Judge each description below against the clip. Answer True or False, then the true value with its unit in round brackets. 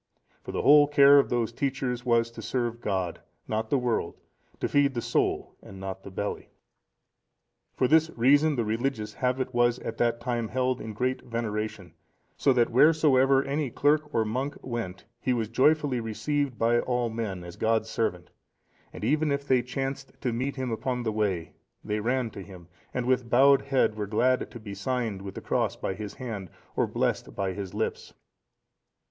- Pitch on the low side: True (120 Hz)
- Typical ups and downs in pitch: True (3.6 semitones)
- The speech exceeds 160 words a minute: True (180 wpm)